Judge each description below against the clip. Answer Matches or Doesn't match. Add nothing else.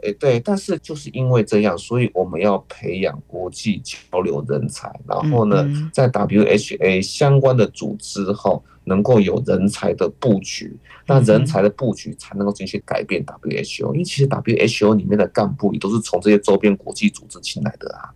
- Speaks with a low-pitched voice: Matches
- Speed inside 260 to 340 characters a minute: Matches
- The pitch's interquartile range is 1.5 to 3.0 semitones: Doesn't match